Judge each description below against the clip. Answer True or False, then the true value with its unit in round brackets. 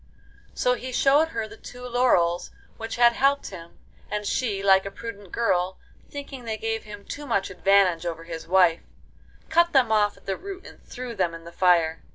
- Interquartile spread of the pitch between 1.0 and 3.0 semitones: False (5.4 semitones)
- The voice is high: True (210 Hz)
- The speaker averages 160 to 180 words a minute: False (195 wpm)